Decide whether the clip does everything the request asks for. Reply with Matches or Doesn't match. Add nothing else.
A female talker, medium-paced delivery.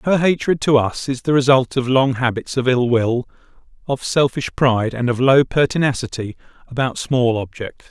Doesn't match